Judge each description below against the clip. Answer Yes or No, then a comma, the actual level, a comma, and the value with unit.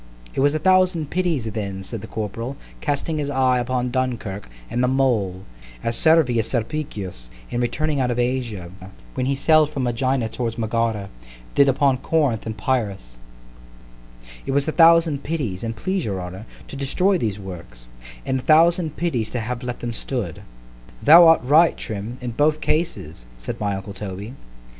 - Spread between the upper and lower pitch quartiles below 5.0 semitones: No, wide, 5.6 semitones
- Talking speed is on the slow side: No, average, 165 wpm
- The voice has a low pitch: Yes, low, 125 Hz